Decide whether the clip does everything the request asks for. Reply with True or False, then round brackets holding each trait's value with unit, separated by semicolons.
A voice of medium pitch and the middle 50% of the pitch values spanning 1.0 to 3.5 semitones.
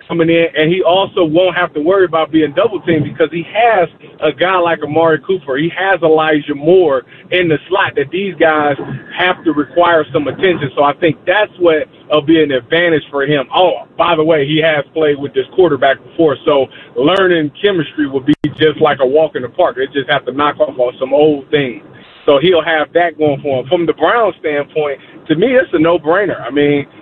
True (155 Hz; 2.8 semitones)